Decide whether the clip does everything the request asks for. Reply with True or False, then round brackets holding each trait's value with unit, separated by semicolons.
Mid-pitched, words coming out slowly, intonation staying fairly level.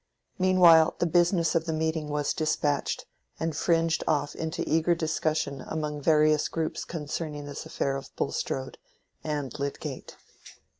True (155 Hz; 130 wpm; 1.9 semitones)